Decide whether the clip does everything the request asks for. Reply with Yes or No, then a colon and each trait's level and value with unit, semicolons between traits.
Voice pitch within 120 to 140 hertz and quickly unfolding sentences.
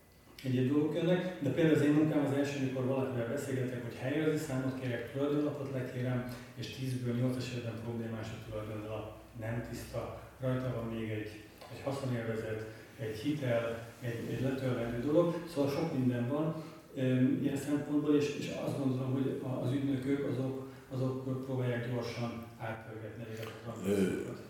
No: low, 130 Hz; average, 140 wpm